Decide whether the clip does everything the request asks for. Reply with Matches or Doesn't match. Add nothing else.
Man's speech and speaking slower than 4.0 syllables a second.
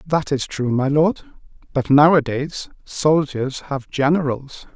Matches